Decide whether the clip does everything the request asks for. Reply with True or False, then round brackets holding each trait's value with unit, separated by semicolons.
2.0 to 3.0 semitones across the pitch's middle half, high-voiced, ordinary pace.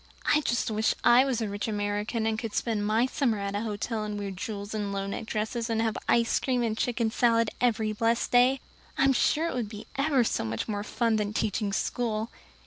False (2.4 semitones; 220 Hz; 220 wpm)